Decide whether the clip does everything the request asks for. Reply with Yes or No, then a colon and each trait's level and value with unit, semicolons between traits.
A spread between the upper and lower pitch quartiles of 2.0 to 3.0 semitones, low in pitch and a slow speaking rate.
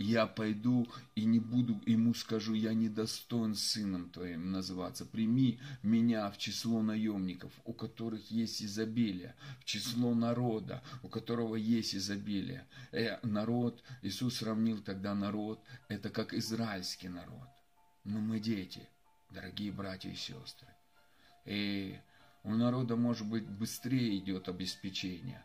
No: average, 2.7 semitones; low, 110 Hz; average, 125 wpm